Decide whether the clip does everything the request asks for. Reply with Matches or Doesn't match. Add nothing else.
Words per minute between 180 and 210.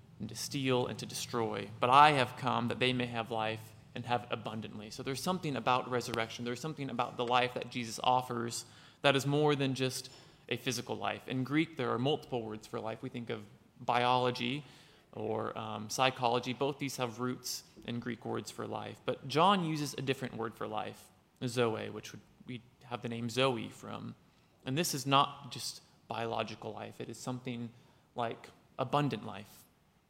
Matches